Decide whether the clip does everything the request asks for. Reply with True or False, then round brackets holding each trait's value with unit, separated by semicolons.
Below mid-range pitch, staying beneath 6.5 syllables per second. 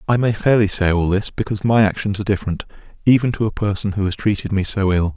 False (100 Hz; 6.7 syllables/s)